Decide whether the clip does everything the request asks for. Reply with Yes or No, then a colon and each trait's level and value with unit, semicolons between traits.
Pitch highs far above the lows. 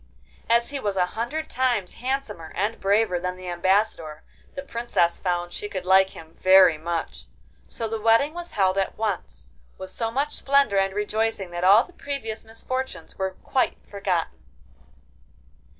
No: average, 4.3 semitones